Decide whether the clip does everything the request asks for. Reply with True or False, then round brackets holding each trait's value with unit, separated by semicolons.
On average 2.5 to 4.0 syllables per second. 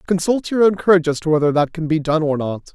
False (6.5 syllables/s)